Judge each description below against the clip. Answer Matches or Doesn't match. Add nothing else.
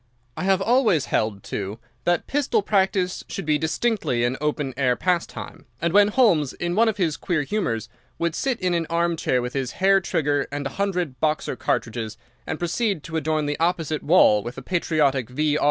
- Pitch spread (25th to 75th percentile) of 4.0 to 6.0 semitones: Matches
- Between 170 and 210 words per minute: Matches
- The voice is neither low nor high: Matches